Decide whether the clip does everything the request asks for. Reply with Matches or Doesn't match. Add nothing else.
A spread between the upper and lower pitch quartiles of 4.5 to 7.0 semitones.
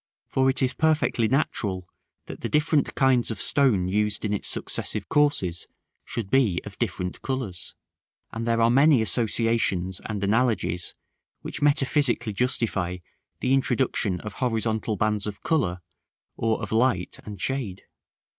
Matches